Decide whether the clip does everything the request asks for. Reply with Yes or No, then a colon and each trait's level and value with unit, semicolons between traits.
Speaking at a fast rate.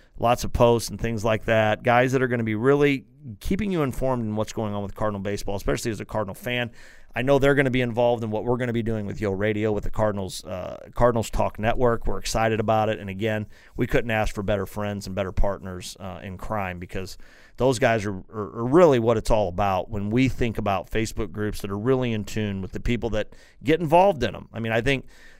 Yes: fast, 265 wpm